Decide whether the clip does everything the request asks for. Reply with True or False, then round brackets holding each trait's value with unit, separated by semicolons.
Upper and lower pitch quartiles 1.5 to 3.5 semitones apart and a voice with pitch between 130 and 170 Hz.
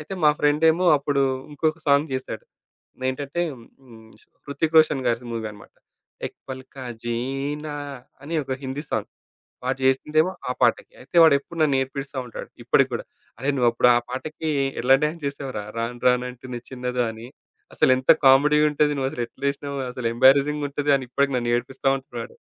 True (2.8 semitones; 135 Hz)